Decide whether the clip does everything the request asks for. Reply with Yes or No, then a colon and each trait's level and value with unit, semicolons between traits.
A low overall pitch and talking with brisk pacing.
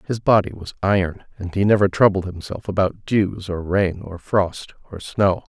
No: very low, 95 Hz; average, 185 wpm